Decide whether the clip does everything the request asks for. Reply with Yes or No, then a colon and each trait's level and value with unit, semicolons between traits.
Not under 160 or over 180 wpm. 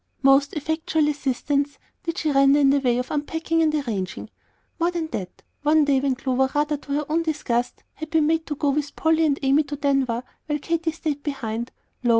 No: average, 200 wpm